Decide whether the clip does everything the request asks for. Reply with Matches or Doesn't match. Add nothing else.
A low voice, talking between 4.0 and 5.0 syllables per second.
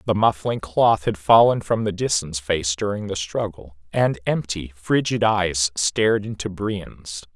Matches